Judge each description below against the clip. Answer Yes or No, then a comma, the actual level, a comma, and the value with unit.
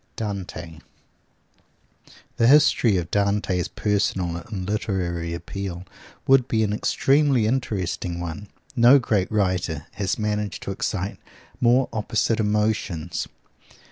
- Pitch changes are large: No, average, 3.6 semitones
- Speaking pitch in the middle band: No, low, 100 Hz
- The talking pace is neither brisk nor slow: No, slow, 110 wpm